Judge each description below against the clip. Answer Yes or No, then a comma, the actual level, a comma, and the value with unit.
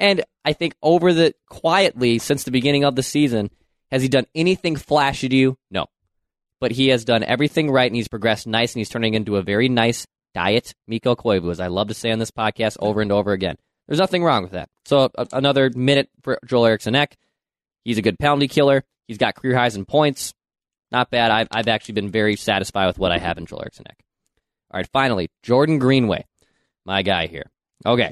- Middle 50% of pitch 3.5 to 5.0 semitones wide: Yes, average, 4.3 semitones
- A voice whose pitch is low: Yes, low, 120 Hz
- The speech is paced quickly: Yes, fast, 215 wpm